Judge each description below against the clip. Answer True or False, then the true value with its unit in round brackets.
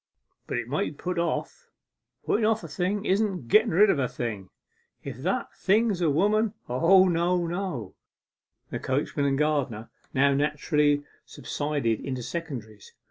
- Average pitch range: False (6.0 semitones)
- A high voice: False (155 Hz)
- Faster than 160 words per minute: False (155 wpm)